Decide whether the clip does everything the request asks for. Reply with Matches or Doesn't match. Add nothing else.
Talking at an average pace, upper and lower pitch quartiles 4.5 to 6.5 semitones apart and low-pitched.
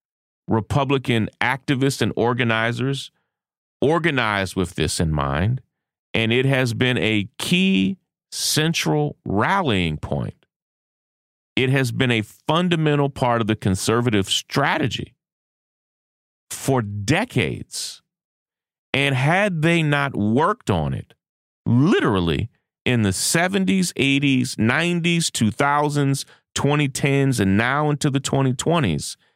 Doesn't match